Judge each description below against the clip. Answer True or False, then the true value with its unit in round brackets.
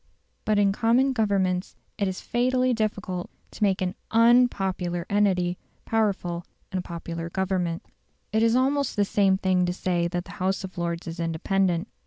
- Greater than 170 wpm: False (165 wpm)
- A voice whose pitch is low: False (190 Hz)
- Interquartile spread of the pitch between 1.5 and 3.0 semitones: False (3.5 semitones)